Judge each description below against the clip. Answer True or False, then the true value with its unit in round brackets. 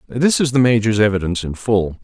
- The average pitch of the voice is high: False (110 Hz)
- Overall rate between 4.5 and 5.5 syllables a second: False (6.0 syllables/s)